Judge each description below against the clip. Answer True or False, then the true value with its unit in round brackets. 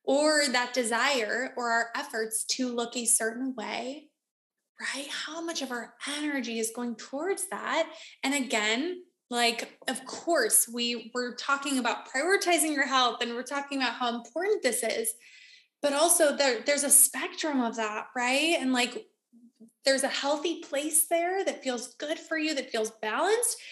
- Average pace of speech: True (165 wpm)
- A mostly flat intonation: False (4.7 semitones)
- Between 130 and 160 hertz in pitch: False (270 Hz)